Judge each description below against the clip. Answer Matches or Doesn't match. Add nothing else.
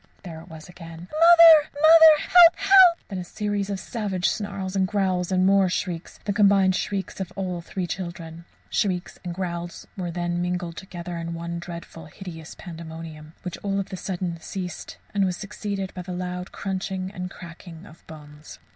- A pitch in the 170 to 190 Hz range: Matches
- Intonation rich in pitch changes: Doesn't match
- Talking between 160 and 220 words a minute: Matches